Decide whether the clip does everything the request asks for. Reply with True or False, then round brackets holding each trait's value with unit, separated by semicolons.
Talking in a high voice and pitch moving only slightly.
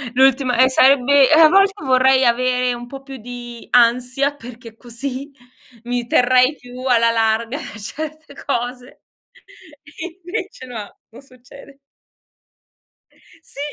True (255 Hz; 2.3 semitones)